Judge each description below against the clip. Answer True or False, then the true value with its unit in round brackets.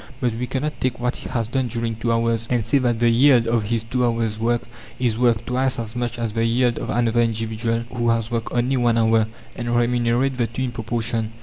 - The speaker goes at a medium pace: False (230 wpm)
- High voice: False (115 Hz)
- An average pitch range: False (1.3 semitones)